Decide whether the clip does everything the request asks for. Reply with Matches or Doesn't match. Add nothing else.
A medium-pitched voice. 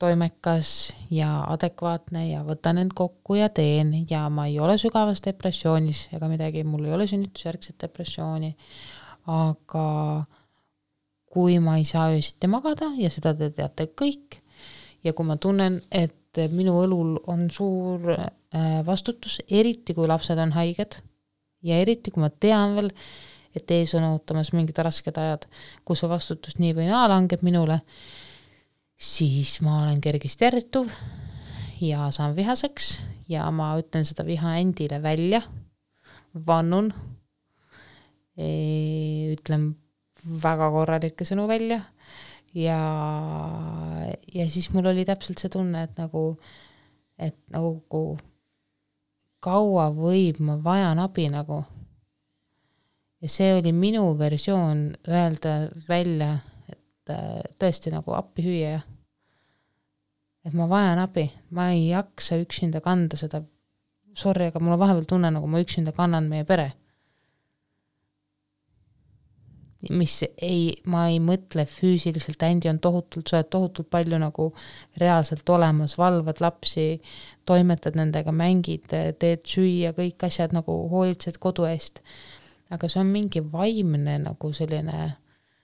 Matches